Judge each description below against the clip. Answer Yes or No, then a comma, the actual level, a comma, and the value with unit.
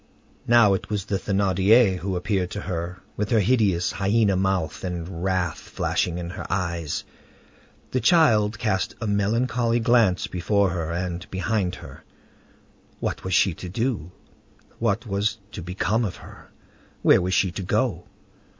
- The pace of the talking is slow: No, average, 150 wpm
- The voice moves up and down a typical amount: Yes, average, 3.2 semitones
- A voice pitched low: Yes, very low, 95 Hz